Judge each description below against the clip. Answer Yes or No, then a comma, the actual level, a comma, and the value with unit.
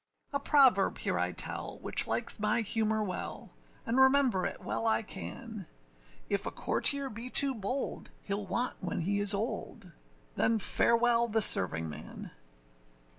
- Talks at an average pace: Yes, average, 145 wpm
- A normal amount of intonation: Yes, average, 3.8 semitones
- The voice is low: No, high, 225 Hz